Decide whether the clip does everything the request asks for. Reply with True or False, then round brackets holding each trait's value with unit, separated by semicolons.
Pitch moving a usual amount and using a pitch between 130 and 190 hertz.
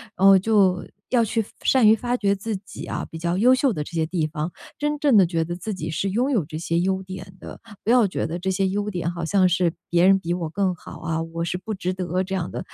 True (3.3 semitones; 185 Hz)